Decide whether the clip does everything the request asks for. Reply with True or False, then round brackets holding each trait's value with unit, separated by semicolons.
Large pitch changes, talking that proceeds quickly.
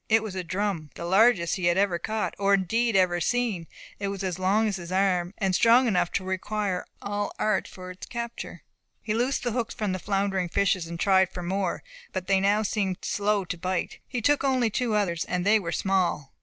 False (2.9 semitones; 220 wpm)